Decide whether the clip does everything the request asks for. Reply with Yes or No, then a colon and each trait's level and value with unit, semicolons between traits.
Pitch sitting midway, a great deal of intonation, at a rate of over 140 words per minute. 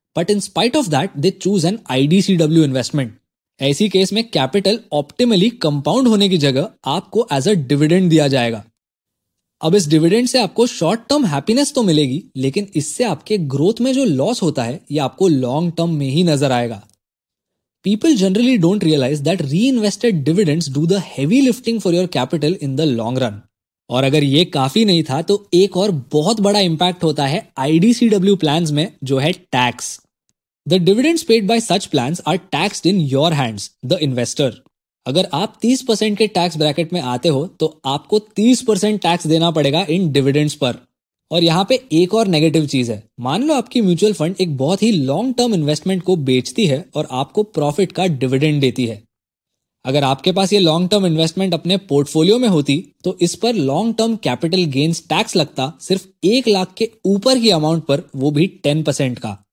Yes: medium, 170 Hz; wide, 6.1 semitones; average, 180 wpm